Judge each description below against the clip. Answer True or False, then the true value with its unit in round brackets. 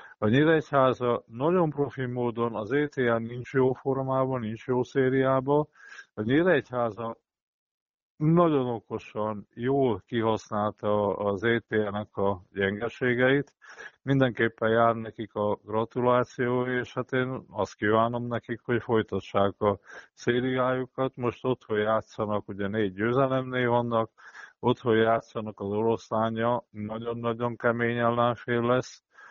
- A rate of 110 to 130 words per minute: True (115 wpm)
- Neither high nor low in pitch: False (120 Hz)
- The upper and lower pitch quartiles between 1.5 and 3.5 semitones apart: True (2.7 semitones)